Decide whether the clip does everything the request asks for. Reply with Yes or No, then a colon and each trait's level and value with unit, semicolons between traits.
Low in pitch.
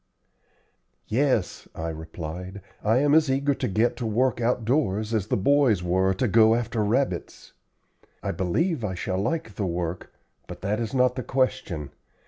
Yes: low, 110 Hz